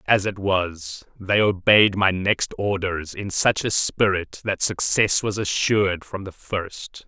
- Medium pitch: No, very low, 95 Hz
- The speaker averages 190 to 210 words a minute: No, average, 160 wpm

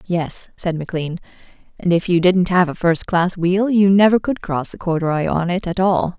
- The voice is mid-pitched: Yes, medium, 180 Hz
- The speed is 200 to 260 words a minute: Yes, fast, 205 wpm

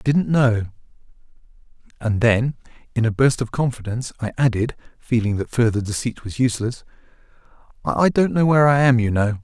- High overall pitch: No, low, 120 Hz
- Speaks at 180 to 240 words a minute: No, average, 165 wpm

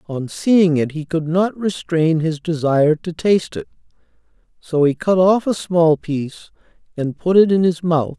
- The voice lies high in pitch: No, medium, 165 Hz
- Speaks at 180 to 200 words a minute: Yes, average, 185 wpm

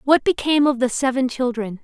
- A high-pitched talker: Yes, very high, 260 Hz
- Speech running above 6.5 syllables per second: No, 5.9 syllables/s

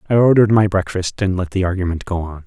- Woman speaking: No, male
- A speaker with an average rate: No, fast, 245 wpm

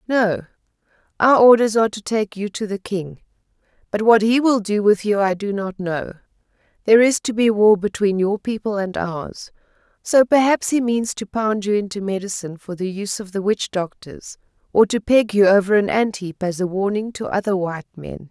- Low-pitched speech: No, high, 205 Hz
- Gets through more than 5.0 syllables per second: Yes, 5.2 syllables/s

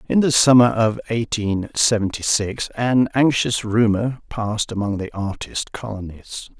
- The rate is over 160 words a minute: No, slow, 135 wpm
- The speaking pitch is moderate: No, low, 110 Hz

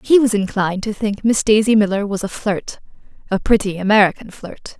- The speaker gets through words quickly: No, average, 175 wpm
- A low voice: No, high, 210 Hz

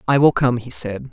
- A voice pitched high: No, low, 125 Hz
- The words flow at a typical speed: No, fast, 270 wpm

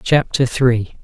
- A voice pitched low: Yes, low, 125 Hz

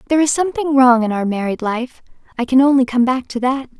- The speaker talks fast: Yes, fast, 220 wpm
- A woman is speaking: Yes, female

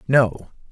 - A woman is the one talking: No, male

